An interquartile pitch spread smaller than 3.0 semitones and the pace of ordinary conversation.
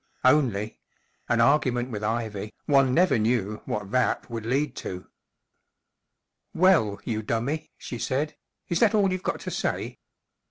No: wide, 5.5 semitones; average, 150 wpm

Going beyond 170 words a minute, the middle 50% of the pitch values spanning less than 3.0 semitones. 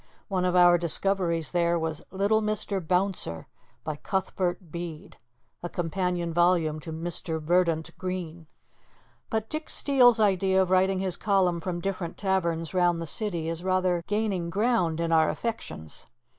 No: average, 145 wpm; narrow, 2.5 semitones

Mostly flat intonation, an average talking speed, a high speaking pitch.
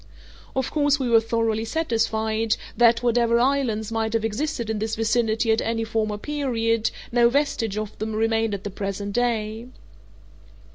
Yes: narrow, 1.5 semitones; average, 155 wpm; high, 225 Hz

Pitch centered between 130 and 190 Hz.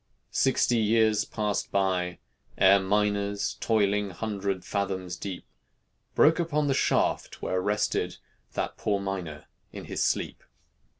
No: low, 100 Hz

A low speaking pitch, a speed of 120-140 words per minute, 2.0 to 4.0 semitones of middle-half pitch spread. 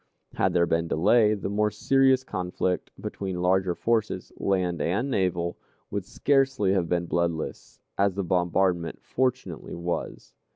Yes: very low, 95 Hz; slow, 135 wpm; average, 3.5 semitones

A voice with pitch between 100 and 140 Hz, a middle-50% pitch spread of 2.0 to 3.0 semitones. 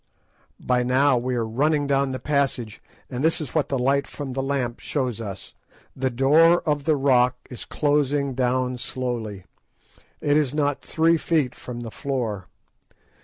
Yes: low, 135 Hz; average, 2.7 semitones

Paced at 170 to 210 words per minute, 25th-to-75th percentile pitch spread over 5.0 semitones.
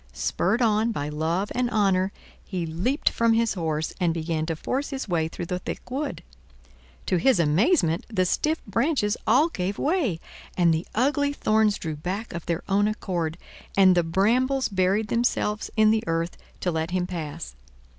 Yes: average, 175 wpm; wide, 5.5 semitones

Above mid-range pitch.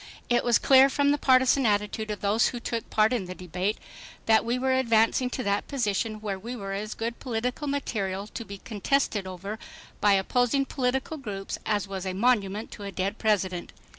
Yes: high, 220 Hz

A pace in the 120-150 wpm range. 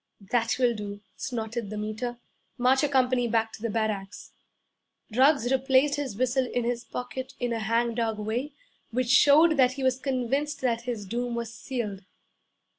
No: average, 165 wpm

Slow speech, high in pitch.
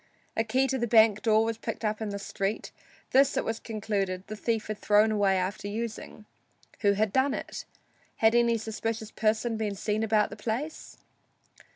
No: average, 185 wpm; high, 220 Hz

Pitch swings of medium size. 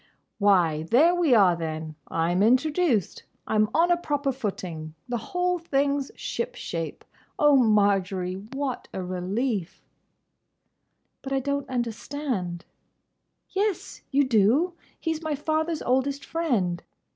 No: wide, 7.7 semitones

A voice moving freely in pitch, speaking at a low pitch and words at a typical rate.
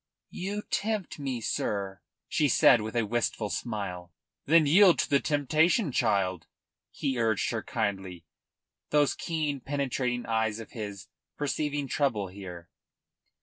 No: wide, 6.2 semitones; low, 120 Hz; slow, 130 wpm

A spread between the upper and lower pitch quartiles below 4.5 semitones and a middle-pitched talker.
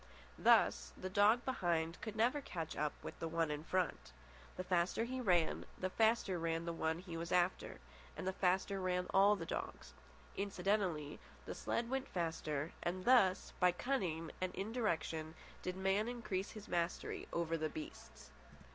Yes: average, 3.6 semitones; medium, 180 Hz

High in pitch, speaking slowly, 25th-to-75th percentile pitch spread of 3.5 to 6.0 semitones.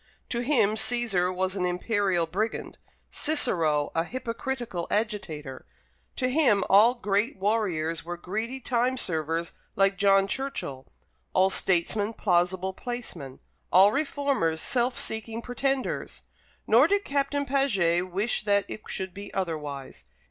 Yes: high, 200 Hz; slow, 125 wpm; wide, 5.5 semitones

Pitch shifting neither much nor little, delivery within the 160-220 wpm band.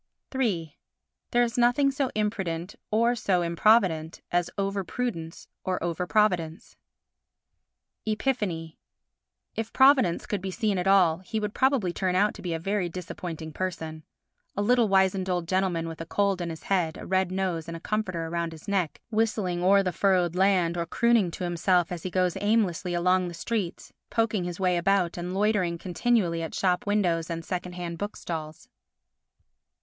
Yes: average, 3.5 semitones; average, 170 wpm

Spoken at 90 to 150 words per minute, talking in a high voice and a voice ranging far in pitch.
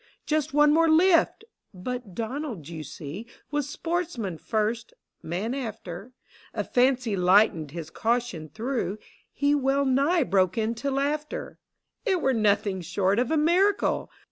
Yes: average, 140 wpm; high, 240 Hz; wide, 6.9 semitones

